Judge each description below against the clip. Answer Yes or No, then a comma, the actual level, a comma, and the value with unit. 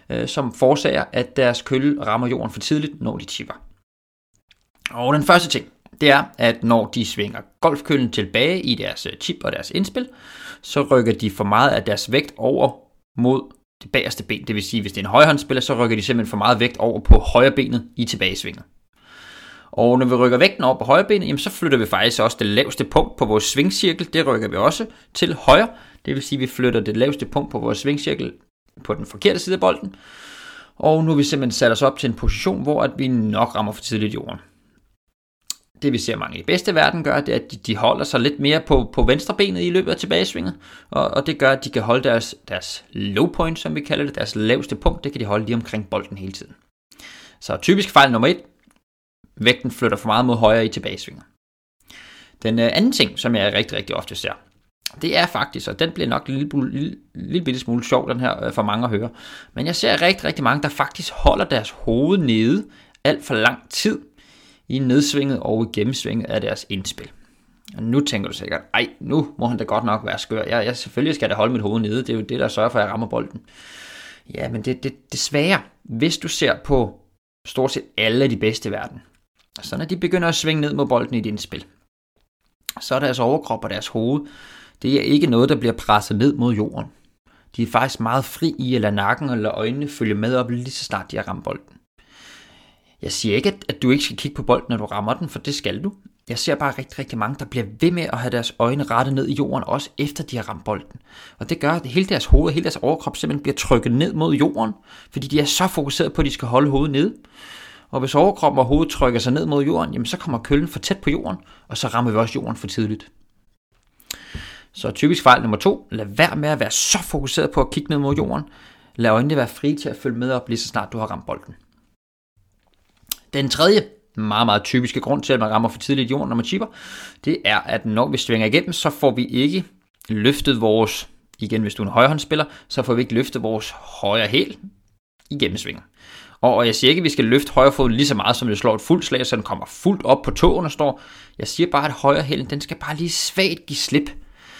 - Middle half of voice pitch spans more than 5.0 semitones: No, average, 4.5 semitones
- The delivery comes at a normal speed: No, fast, 235 wpm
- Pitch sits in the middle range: No, low, 130 Hz